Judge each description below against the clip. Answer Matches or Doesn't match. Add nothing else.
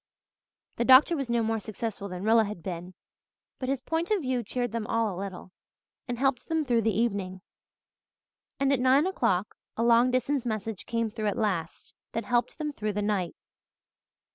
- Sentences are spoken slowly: Doesn't match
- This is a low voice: Doesn't match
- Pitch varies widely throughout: Doesn't match